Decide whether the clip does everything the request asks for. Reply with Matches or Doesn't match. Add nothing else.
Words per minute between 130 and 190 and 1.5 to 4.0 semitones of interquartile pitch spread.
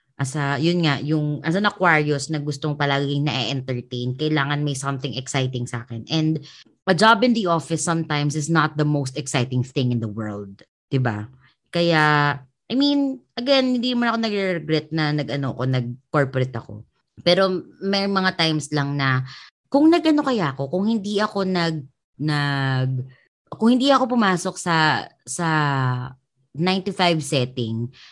Doesn't match